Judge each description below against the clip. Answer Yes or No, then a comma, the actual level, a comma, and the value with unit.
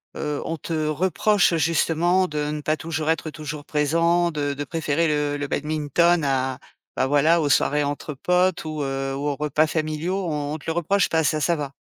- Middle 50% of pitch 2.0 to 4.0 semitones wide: Yes, narrow, 2.4 semitones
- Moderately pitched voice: Yes, medium, 155 Hz